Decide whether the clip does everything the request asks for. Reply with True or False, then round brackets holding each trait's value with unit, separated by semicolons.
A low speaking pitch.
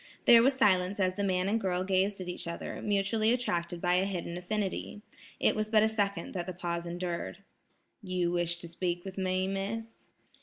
False (185 Hz)